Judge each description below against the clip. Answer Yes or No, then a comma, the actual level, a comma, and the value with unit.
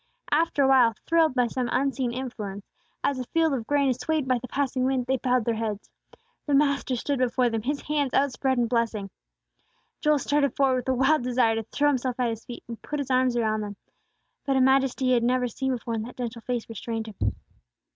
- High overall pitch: Yes, very high, 255 Hz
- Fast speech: Yes, fast, 215 wpm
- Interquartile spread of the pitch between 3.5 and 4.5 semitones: No, narrow, 2.6 semitones